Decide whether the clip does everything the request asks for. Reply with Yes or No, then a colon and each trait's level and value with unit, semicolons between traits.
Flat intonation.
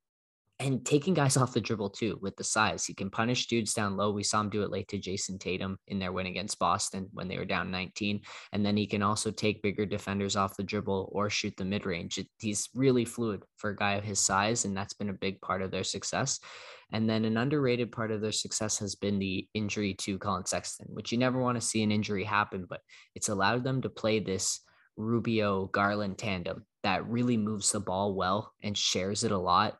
Yes: narrow, 2.3 semitones